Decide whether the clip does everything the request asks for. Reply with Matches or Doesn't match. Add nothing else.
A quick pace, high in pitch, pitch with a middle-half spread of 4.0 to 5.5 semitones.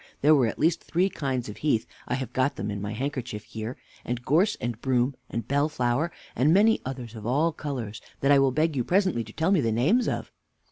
Doesn't match